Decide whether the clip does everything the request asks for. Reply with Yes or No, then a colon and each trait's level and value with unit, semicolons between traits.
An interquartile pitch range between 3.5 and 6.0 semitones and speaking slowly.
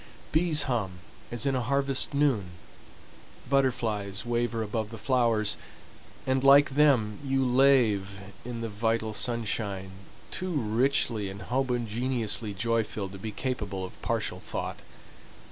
Yes: average, 4.1 semitones; slow, 130 wpm